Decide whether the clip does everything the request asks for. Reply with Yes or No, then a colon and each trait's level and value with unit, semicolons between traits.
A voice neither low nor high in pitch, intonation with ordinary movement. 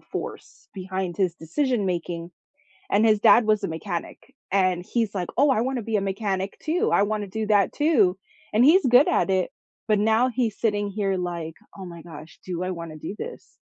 No: high, 200 Hz; average, 3.8 semitones